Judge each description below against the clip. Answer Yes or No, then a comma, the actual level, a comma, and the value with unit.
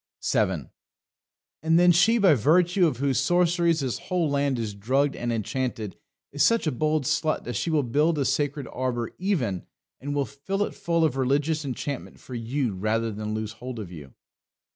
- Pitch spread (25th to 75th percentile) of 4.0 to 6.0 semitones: Yes, average, 5.3 semitones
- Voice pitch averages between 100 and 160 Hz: Yes, medium, 140 Hz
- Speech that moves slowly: No, average, 185 wpm